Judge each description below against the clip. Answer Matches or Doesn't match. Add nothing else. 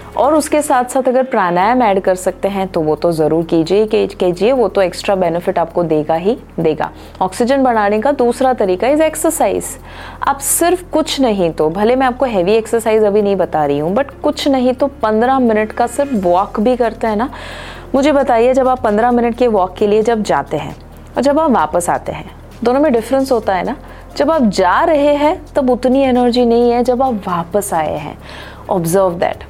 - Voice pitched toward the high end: Matches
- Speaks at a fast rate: Matches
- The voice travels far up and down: Matches